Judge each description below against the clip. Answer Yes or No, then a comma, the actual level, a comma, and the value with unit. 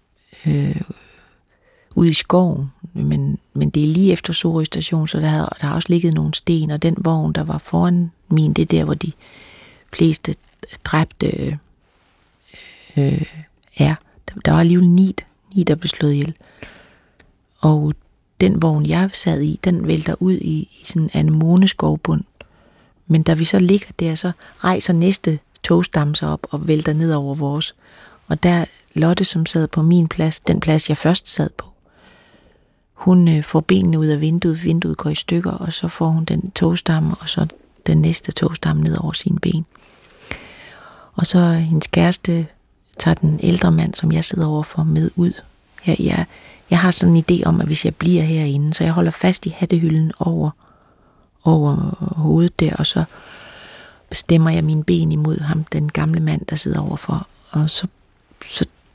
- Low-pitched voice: No, medium, 165 Hz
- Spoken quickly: No, average, 175 wpm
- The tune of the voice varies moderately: No, narrow, 2.2 semitones